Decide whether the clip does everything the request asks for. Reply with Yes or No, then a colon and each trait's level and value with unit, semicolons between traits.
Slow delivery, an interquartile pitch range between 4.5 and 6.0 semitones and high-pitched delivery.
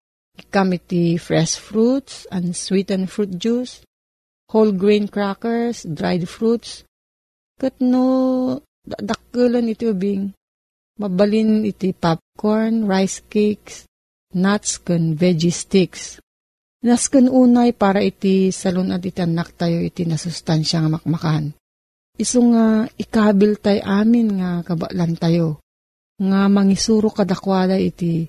No: slow, 105 wpm; average, 4.0 semitones; high, 195 Hz